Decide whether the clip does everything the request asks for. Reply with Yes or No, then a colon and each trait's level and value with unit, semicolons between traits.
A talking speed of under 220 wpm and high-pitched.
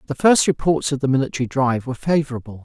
No: fast, 205 wpm; low, 135 Hz